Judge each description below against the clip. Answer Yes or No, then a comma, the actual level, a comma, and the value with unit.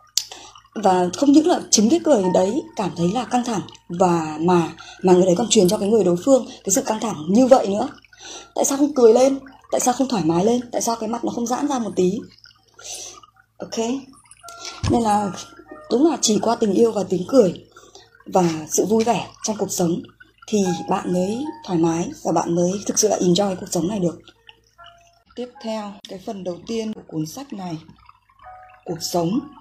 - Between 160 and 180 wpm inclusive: No, average, 205 wpm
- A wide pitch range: Yes, wide, 6.6 semitones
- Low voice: No, high, 220 Hz